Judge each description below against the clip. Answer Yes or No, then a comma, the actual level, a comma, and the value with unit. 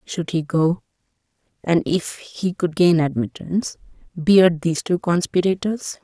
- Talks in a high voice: No, medium, 170 Hz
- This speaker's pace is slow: Yes, slow, 110 wpm